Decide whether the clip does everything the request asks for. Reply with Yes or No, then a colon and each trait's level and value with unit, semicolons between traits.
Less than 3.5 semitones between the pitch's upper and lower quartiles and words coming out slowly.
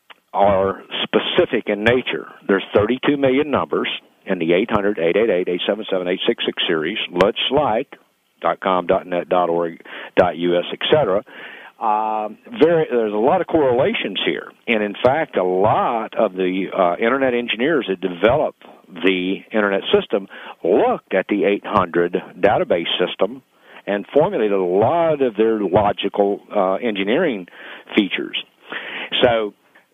No: average, 4.3 semitones; slow, 120 wpm